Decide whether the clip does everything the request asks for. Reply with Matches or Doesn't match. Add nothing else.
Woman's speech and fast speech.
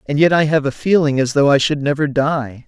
Doesn't match